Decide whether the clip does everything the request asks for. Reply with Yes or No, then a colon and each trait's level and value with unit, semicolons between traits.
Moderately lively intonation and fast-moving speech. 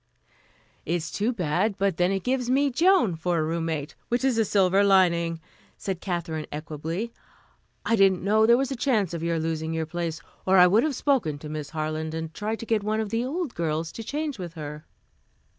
No: wide, 5.8 semitones; fast, 210 wpm